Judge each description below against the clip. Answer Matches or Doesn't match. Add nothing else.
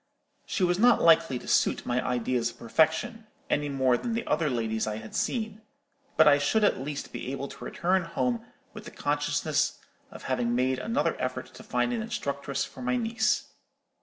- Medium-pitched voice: Matches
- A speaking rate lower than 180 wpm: Doesn't match